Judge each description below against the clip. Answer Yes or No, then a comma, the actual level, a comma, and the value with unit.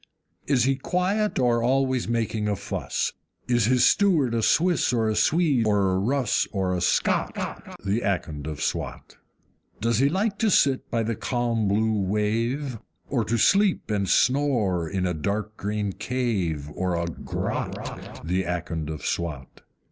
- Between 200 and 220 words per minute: No, average, 160 wpm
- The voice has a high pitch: No, low, 110 Hz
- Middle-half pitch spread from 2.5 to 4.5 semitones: No, wide, 5.5 semitones